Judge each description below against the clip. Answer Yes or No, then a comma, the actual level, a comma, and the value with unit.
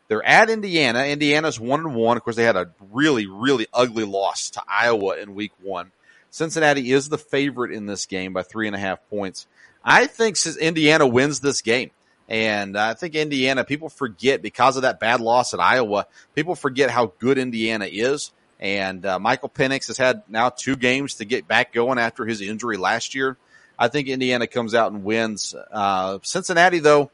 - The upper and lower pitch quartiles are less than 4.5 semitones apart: No, average, 4.8 semitones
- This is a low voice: Yes, low, 125 Hz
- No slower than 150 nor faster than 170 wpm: No, average, 190 wpm